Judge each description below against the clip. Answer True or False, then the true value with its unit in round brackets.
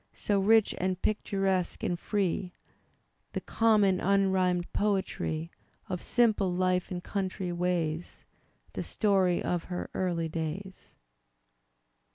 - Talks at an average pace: False (110 wpm)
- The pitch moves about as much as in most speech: False (2.0 semitones)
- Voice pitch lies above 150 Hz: True (185 Hz)